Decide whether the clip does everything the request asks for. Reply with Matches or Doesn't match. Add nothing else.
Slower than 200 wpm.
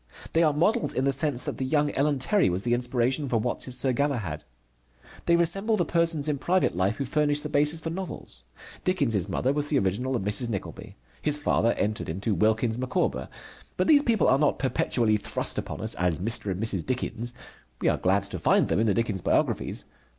Doesn't match